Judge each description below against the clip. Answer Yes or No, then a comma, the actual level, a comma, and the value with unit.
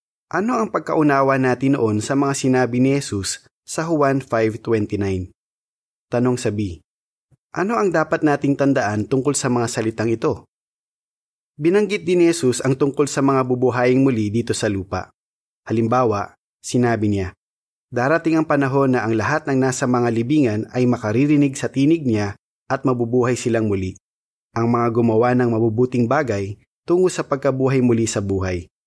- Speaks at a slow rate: No, average, 150 wpm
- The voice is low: Yes, low, 125 Hz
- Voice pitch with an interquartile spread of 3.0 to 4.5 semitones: Yes, average, 3.7 semitones